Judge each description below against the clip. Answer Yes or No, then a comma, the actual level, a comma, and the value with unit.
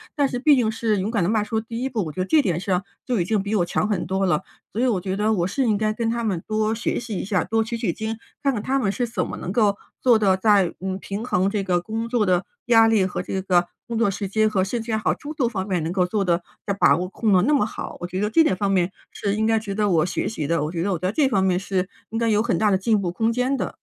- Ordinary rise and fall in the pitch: Yes, average, 3.3 semitones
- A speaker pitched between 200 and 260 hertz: Yes, high, 210 Hz